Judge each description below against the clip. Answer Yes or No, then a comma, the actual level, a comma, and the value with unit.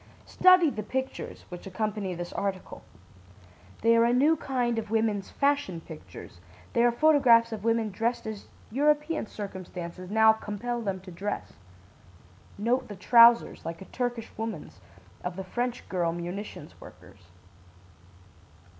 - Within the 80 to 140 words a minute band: Yes, slow, 135 wpm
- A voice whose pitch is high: Yes, high, 220 Hz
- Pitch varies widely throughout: No, average, 4.4 semitones